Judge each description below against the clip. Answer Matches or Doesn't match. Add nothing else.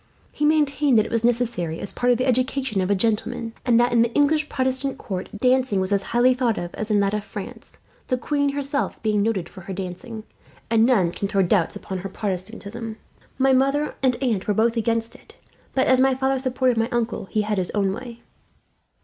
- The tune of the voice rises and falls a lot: Doesn't match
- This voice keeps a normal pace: Doesn't match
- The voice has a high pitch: Matches